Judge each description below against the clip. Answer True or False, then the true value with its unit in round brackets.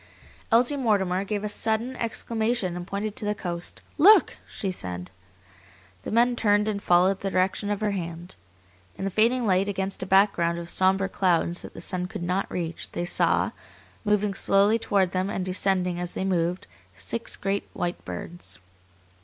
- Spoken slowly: False (170 wpm)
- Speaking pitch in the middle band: False (195 Hz)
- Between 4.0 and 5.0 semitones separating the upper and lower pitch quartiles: False (2.9 semitones)